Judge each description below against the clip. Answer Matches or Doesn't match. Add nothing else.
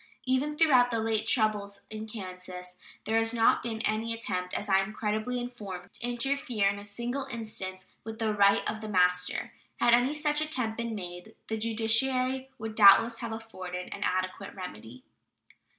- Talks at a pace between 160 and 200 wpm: Matches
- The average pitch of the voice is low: Doesn't match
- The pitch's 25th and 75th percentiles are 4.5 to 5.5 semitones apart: Doesn't match